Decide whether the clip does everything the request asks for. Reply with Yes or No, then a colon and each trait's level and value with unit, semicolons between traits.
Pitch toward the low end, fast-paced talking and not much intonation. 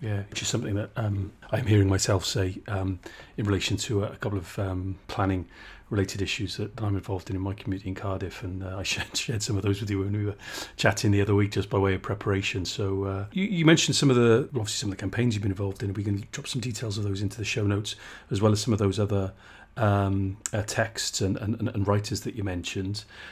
Yes: low, 100 Hz; fast, 260 wpm; narrow, 2.0 semitones